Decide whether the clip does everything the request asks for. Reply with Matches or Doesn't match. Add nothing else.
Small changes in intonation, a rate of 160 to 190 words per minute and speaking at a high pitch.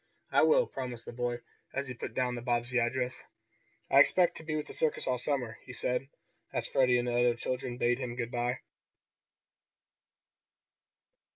Doesn't match